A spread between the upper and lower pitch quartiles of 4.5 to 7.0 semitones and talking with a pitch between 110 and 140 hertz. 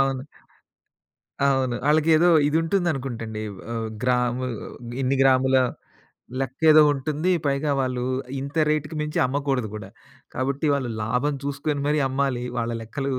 No: average, 2.9 semitones; low, 135 Hz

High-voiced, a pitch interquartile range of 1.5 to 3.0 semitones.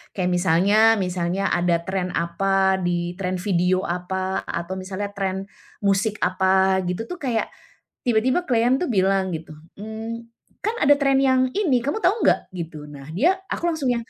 No: high, 195 Hz; average, 4.9 semitones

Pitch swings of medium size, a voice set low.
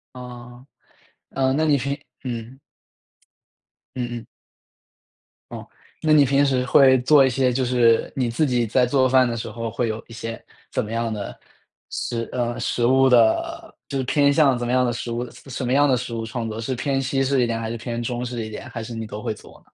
No: narrow, 2.3 semitones; low, 125 Hz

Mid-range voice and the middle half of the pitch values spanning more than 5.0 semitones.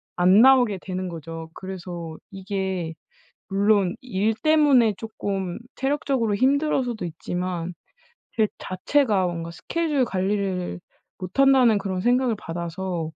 No: high, 195 Hz; wide, 5.5 semitones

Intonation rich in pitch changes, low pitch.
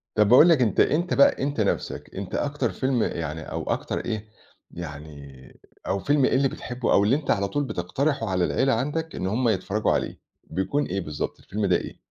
Yes: wide, 6.9 semitones; low, 110 Hz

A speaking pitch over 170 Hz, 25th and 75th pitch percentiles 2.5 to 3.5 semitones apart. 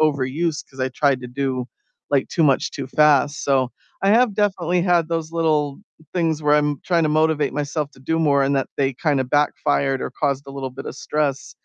No: medium, 145 Hz; average, 2.8 semitones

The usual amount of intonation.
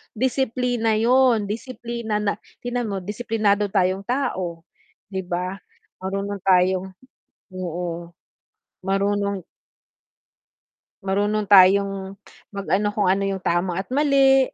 Yes: average, 3.1 semitones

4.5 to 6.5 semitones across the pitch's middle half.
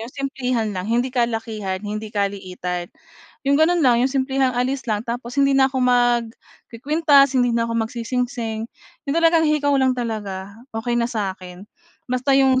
No: average, 3.4 semitones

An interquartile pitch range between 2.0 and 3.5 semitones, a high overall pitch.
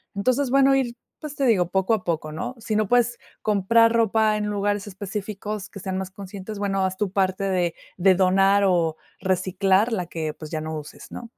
Yes: narrow, 2.6 semitones; high, 195 Hz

